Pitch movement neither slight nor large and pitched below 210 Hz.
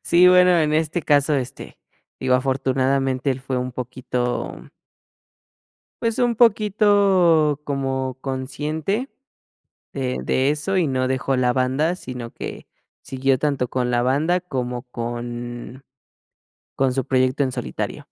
Yes: average, 3.7 semitones; low, 135 Hz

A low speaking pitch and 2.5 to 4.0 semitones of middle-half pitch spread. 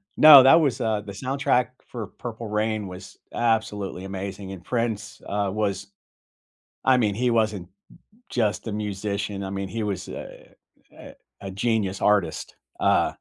Yes: low, 105 Hz; average, 2.8 semitones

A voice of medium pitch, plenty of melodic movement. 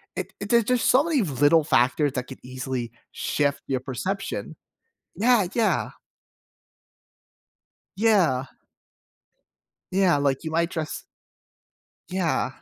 Yes: medium, 160 Hz; wide, 7.1 semitones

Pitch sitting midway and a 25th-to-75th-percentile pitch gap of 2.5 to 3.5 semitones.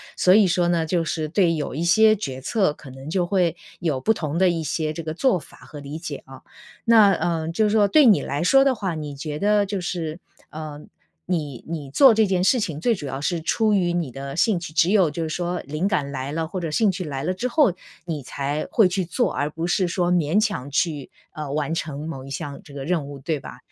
No: medium, 165 Hz; average, 4.2 semitones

